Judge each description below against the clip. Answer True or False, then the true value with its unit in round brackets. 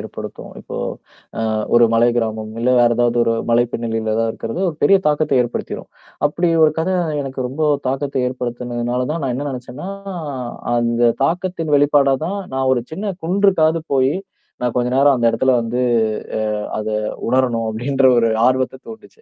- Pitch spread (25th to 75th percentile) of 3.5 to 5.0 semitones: True (3.8 semitones)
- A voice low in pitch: True (130 Hz)